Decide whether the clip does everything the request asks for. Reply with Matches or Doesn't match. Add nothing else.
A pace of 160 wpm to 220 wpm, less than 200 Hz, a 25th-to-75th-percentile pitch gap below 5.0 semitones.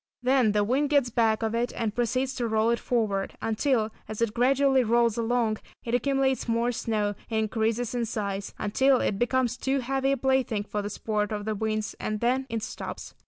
Doesn't match